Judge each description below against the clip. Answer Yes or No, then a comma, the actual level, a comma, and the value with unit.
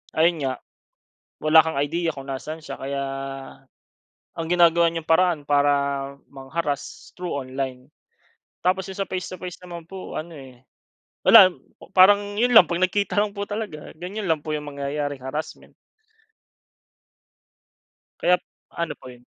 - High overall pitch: No, medium, 165 Hz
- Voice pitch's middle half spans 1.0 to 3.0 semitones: No, average, 4.4 semitones